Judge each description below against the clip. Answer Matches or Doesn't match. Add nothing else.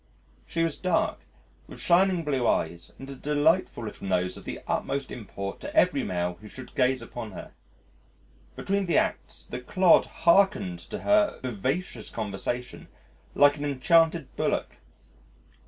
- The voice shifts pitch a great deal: Matches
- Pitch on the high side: Doesn't match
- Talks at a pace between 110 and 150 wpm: Matches